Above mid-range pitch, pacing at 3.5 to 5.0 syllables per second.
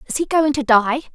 No: very high, 270 Hz; 6.1 syllables/s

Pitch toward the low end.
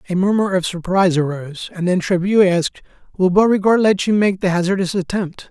No: medium, 185 Hz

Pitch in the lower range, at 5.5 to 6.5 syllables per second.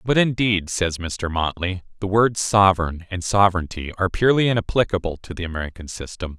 Yes: very low, 95 Hz; 5.8 syllables/s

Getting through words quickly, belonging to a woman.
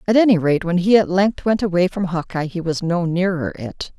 Yes: fast, 240 wpm; female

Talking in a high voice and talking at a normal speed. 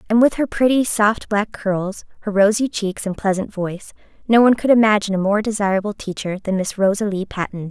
Yes: high, 205 Hz; average, 195 wpm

